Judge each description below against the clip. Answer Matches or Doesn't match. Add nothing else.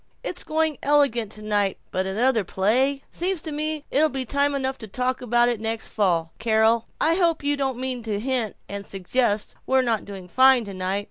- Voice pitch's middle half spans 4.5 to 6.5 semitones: Matches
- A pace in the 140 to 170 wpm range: Doesn't match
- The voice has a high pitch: Matches